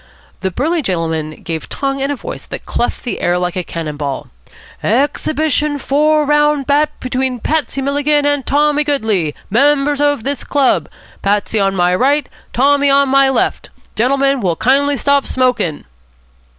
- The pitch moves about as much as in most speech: No, wide, 5.7 semitones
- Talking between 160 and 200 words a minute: Yes, average, 170 wpm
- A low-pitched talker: No, very high, 275 Hz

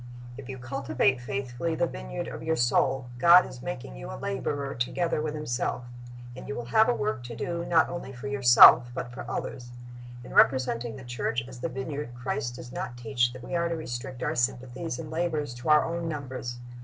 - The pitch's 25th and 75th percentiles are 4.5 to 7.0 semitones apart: No, average, 3.9 semitones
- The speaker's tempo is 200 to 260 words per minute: Yes, fast, 205 wpm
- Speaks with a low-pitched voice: Yes, low, 130 Hz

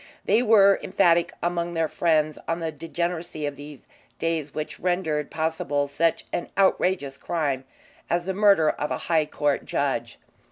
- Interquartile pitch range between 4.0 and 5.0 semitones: No, average, 2.7 semitones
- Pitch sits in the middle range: Yes, medium, 165 Hz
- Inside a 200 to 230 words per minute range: No, average, 155 wpm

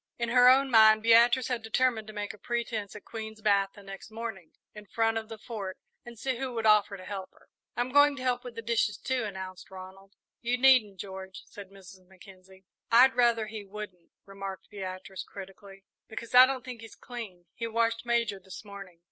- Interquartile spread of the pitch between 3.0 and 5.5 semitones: Yes, average, 3.4 semitones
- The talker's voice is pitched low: No, high, 215 Hz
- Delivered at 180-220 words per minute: Yes, average, 200 wpm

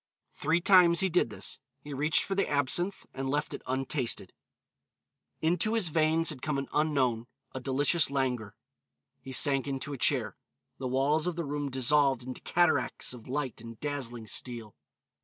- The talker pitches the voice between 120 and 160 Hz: Yes, medium, 140 Hz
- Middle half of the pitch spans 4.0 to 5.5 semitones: No, average, 3.6 semitones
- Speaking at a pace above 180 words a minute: No, average, 165 wpm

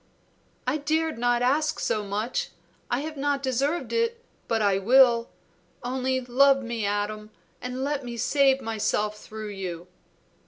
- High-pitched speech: Yes, very high, 250 Hz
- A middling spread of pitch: Yes, average, 4.5 semitones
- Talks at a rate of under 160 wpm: Yes, average, 145 wpm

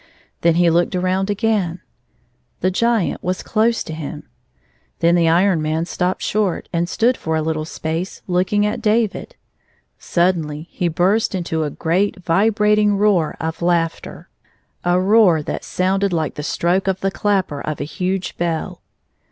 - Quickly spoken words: No, average, 160 wpm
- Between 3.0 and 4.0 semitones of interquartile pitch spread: Yes, average, 3.5 semitones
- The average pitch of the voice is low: No, medium, 180 Hz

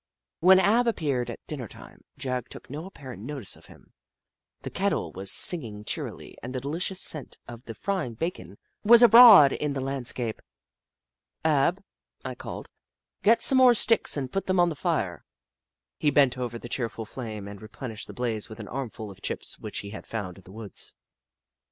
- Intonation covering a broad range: Yes, wide, 7.5 semitones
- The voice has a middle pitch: No, low, 130 Hz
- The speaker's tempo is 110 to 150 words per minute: No, average, 190 wpm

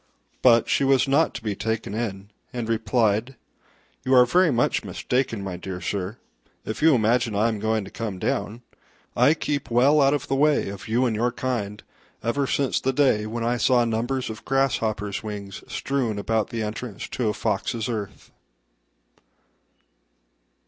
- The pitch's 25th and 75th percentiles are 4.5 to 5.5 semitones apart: No, average, 3.5 semitones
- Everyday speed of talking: Yes, average, 170 wpm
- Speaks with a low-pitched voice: Yes, low, 115 Hz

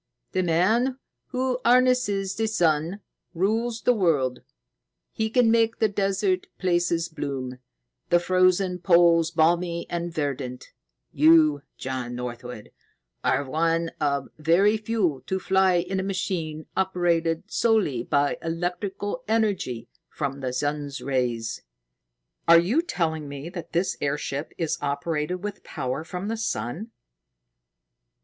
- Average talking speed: No, slow, 125 wpm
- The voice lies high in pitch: No, medium, 170 Hz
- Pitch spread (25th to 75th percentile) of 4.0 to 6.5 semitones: Yes, average, 5.2 semitones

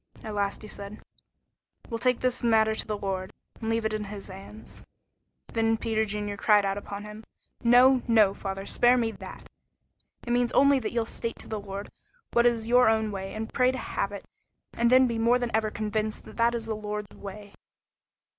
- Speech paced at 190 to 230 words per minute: Yes, average, 200 wpm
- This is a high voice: Yes, high, 220 Hz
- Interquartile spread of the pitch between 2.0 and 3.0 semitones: Yes, narrow, 2.4 semitones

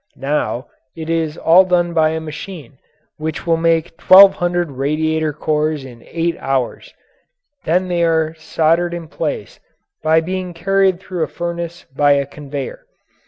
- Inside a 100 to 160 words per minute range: Yes, average, 150 wpm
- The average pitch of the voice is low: No, medium, 160 Hz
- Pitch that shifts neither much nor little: No, narrow, 2.3 semitones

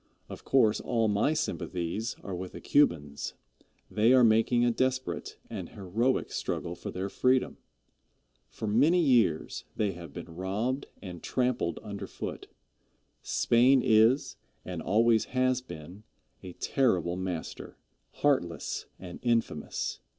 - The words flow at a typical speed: No, slow, 130 wpm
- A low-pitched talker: Yes, low, 110 Hz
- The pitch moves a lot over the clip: Yes, wide, 5.9 semitones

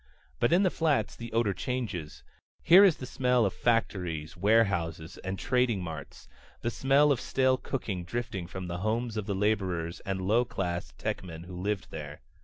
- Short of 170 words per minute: No, average, 175 wpm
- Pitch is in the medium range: No, low, 100 Hz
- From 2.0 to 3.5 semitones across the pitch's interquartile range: No, wide, 5.6 semitones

